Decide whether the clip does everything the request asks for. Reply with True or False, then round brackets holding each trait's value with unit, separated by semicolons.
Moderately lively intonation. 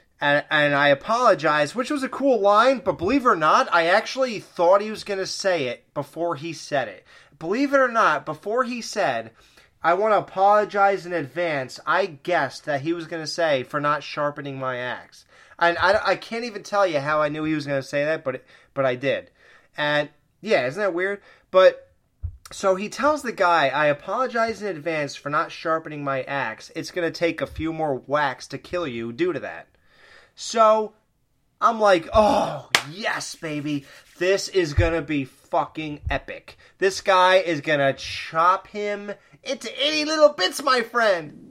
False (6.4 semitones)